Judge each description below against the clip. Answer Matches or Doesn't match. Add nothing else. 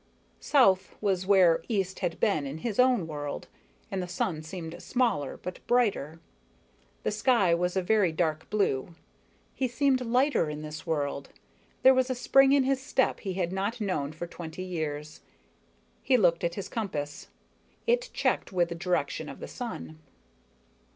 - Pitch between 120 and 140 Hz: Doesn't match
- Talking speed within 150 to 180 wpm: Matches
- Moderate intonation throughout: Doesn't match